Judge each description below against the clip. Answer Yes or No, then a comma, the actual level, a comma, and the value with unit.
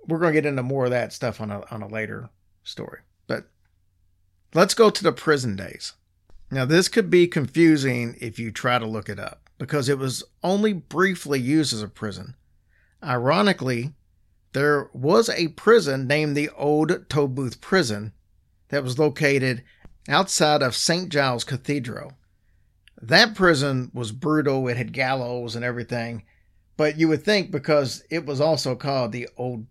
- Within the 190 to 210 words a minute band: No, average, 165 wpm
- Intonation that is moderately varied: No, wide, 5.8 semitones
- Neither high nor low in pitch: No, low, 130 Hz